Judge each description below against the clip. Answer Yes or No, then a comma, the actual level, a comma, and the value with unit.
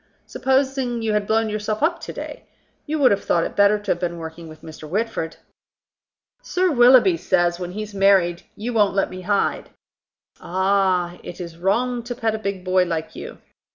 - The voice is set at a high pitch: Yes, high, 200 Hz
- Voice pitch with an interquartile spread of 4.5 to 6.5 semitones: Yes, average, 4.8 semitones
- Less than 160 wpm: No, average, 190 wpm